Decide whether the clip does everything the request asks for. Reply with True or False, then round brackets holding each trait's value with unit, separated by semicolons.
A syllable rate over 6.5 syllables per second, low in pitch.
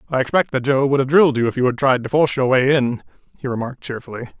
True (7.4 syllables/s; 130 Hz)